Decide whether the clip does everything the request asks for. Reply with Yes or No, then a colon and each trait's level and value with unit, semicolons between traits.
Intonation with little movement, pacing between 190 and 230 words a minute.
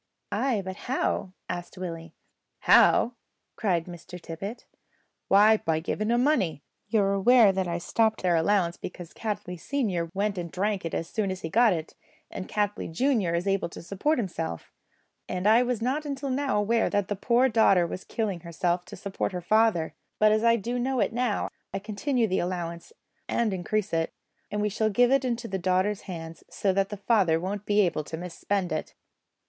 No: average, 4.3 semitones; average, 195 wpm